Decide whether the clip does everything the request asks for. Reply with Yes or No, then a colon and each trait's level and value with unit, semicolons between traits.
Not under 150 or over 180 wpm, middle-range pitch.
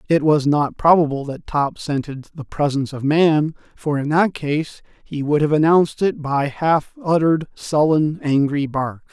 Yes: average, 170 wpm; medium, 150 Hz